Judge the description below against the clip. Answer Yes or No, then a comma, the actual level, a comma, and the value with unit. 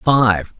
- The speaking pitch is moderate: No, low, 110 Hz